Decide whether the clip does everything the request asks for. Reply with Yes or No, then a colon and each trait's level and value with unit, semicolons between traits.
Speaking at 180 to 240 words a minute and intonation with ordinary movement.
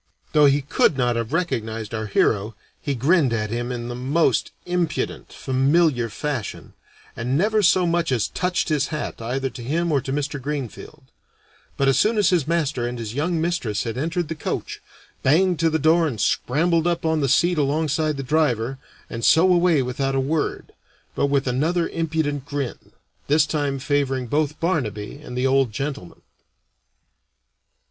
No: average, 170 wpm; average, 4.5 semitones